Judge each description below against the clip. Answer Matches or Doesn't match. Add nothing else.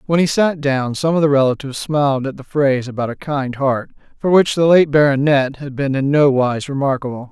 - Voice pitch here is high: Doesn't match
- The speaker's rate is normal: Doesn't match